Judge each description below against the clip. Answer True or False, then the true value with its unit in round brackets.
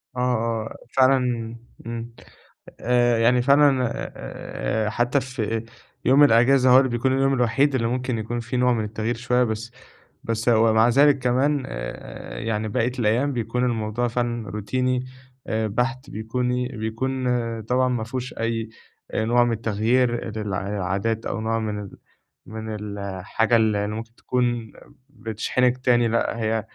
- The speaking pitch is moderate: False (115 Hz)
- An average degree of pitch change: False (2.2 semitones)